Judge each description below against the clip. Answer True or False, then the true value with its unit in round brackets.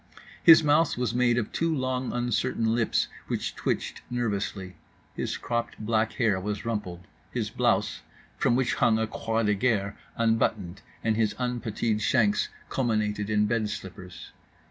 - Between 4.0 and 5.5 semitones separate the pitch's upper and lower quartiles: False (2.6 semitones)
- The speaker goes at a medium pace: True (145 wpm)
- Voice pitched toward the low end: True (110 Hz)